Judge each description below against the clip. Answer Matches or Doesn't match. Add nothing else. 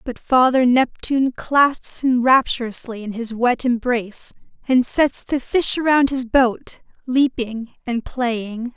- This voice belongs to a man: Doesn't match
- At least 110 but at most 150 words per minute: Matches